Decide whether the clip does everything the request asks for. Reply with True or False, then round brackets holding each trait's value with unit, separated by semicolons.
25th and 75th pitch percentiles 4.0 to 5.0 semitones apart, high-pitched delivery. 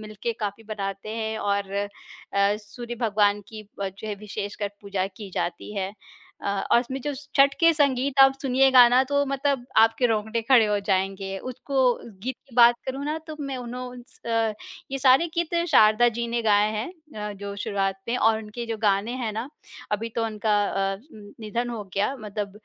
False (3.6 semitones; 225 Hz)